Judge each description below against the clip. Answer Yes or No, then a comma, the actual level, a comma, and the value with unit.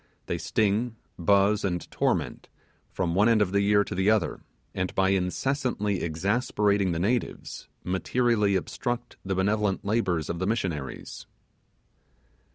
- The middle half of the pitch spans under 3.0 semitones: Yes, narrow, 2.6 semitones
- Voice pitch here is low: Yes, low, 100 Hz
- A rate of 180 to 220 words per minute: No, slow, 135 wpm